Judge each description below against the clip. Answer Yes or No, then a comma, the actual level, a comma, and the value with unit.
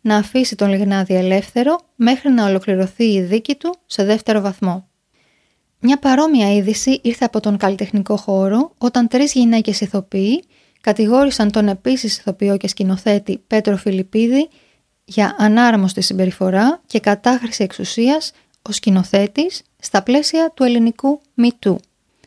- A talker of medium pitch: No, high, 215 Hz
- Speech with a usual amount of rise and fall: Yes, average, 4.3 semitones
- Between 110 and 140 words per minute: Yes, average, 125 wpm